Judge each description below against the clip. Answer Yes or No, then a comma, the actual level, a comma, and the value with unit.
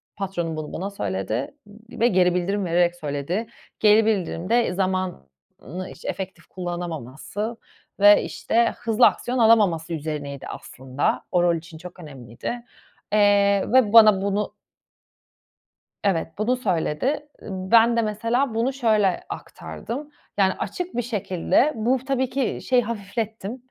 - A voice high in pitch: Yes, high, 200 Hz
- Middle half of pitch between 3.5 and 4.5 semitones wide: No, average, 4.9 semitones